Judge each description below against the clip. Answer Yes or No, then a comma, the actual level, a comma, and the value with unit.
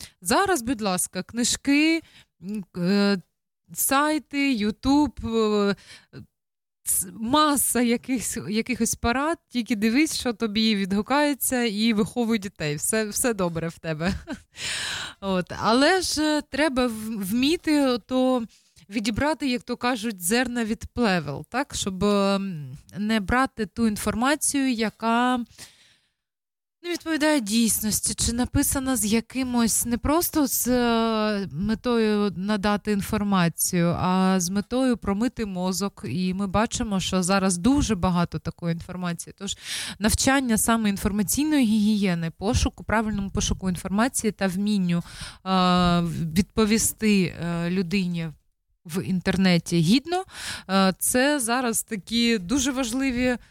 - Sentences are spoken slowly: Yes, slow, 105 wpm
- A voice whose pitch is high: Yes, high, 220 Hz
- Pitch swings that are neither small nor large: Yes, average, 4.7 semitones